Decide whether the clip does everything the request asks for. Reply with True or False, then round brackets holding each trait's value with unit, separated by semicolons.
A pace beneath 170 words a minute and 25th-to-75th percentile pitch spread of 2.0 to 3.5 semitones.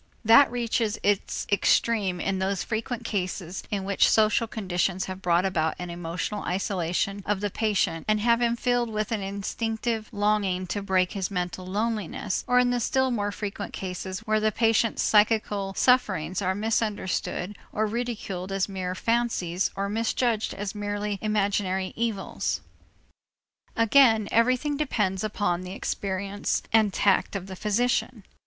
True (150 wpm; 3.0 semitones)